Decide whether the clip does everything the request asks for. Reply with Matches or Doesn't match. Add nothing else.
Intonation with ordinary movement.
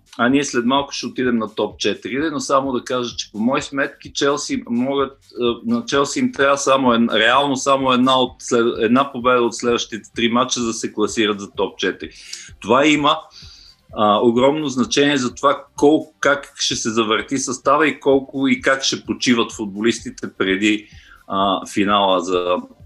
Matches